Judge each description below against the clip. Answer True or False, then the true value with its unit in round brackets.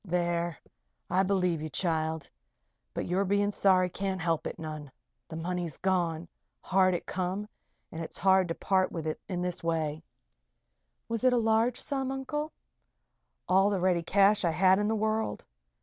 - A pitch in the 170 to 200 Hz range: True (185 Hz)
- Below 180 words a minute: True (165 wpm)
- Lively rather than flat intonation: False (3.2 semitones)